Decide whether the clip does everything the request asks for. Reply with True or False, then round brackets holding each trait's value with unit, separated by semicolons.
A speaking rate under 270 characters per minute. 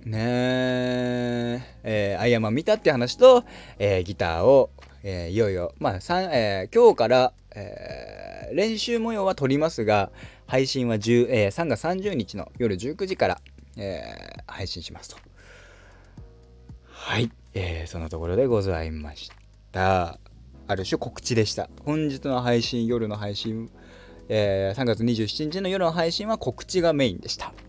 True (260 characters per minute)